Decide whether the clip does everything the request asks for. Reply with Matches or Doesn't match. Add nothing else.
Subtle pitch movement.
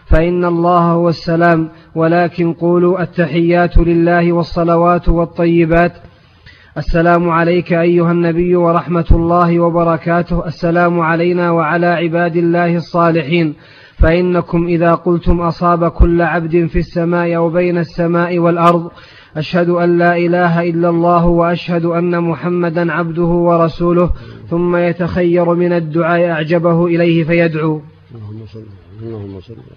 Matches